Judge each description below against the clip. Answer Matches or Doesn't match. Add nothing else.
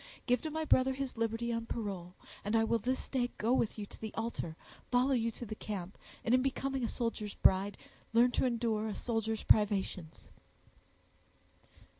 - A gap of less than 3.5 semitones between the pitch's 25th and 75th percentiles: Matches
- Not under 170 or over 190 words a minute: Matches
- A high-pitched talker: Matches